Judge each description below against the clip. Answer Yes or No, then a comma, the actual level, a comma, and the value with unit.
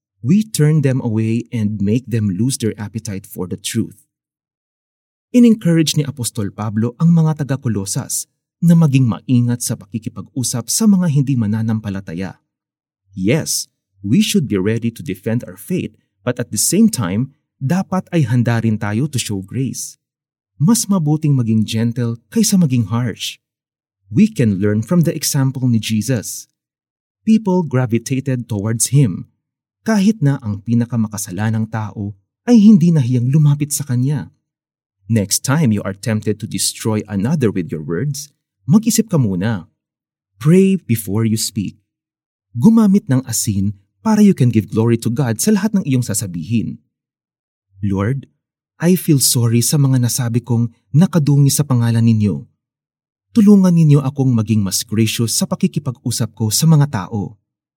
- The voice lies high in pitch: No, low, 120 Hz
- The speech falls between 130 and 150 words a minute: Yes, average, 145 wpm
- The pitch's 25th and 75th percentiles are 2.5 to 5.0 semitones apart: No, wide, 5.5 semitones